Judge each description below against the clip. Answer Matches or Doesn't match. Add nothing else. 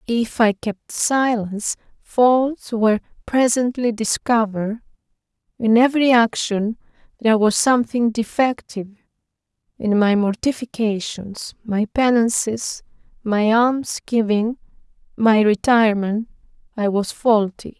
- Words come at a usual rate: Doesn't match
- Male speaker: Doesn't match